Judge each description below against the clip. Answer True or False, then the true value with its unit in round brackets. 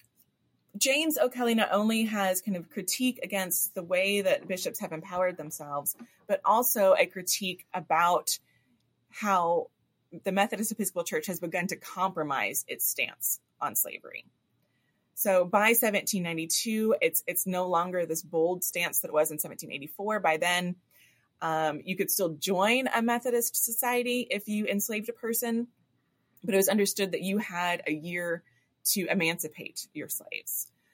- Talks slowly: False (150 wpm)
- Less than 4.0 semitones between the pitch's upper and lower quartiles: False (4.3 semitones)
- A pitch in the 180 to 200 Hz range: True (190 Hz)